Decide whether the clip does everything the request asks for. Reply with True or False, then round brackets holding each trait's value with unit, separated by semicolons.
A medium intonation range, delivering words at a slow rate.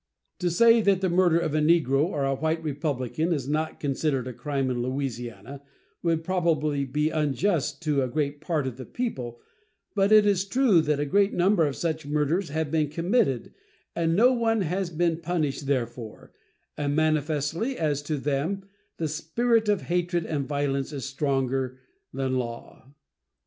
False (4.0 semitones; 170 wpm)